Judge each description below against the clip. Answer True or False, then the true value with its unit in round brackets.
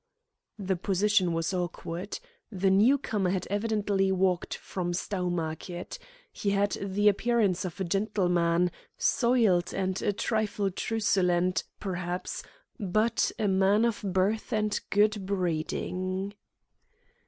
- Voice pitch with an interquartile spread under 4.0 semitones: True (2.5 semitones)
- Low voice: False (195 Hz)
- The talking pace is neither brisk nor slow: False (115 wpm)